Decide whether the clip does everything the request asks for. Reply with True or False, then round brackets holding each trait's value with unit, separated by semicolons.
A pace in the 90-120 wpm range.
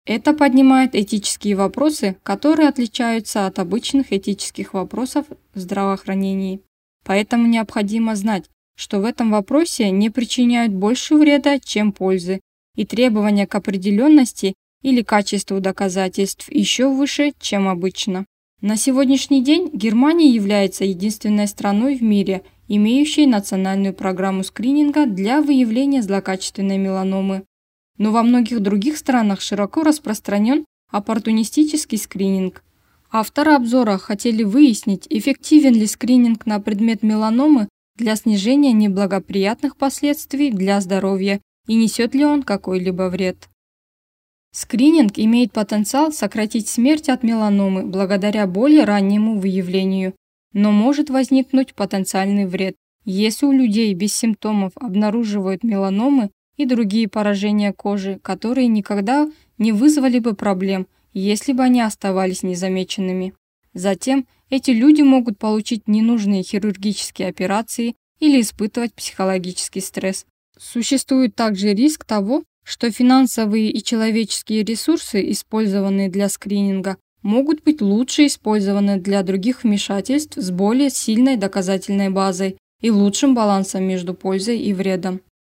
True (115 wpm)